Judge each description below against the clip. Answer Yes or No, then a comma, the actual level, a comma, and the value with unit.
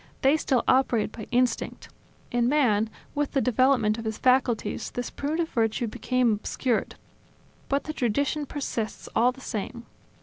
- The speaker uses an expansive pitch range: No, average, 3.3 semitones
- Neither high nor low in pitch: No, very high, 250 Hz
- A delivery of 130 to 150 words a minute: Yes, average, 145 wpm